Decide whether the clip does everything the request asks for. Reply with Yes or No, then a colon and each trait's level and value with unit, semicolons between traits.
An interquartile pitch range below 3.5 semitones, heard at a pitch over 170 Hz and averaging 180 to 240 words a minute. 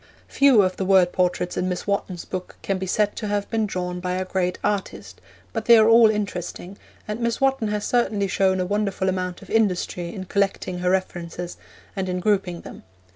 Yes: narrow, 2.6 semitones; high, 190 Hz; average, 200 wpm